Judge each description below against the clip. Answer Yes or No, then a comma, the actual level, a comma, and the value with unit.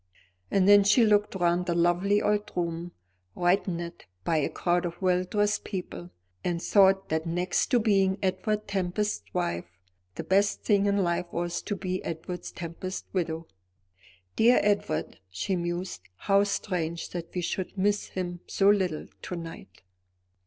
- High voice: No, medium, 180 Hz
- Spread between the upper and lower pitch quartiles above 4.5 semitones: No, narrow, 2.6 semitones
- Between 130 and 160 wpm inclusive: Yes, average, 150 wpm